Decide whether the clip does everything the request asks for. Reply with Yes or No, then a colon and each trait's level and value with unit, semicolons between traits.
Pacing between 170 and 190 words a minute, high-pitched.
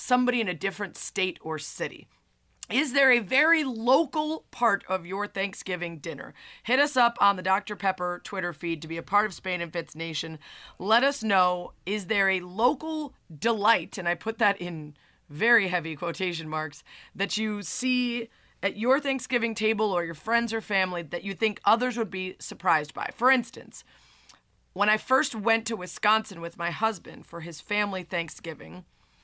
Yes: average, 180 wpm; high, 200 Hz